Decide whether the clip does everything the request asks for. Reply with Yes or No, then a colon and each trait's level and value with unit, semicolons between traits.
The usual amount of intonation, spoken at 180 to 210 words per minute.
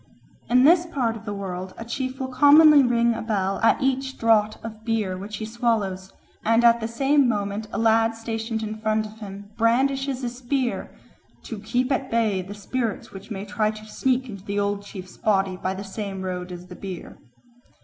Yes: average, 3.5 semitones; average, 200 wpm